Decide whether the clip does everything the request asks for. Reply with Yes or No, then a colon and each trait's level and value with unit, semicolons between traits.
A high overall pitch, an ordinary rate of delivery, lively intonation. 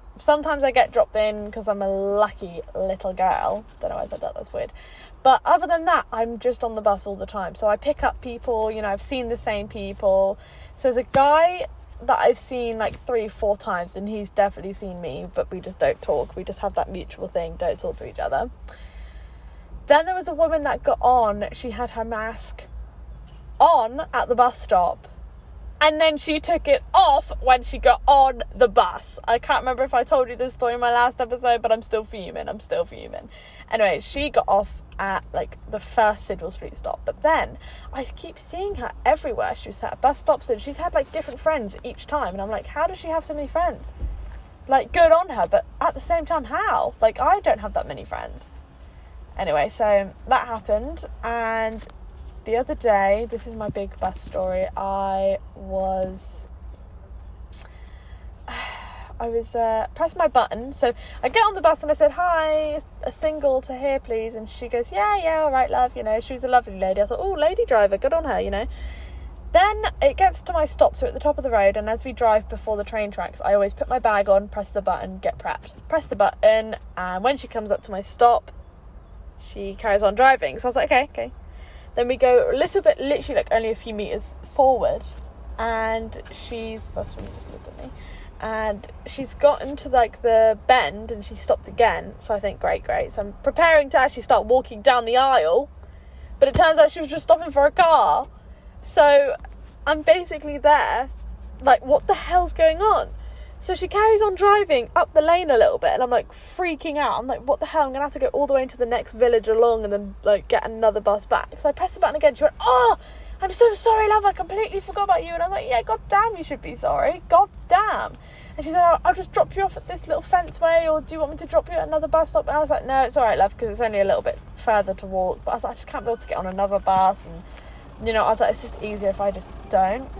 No: very high, 250 Hz; fast, 235 wpm; wide, 7.4 semitones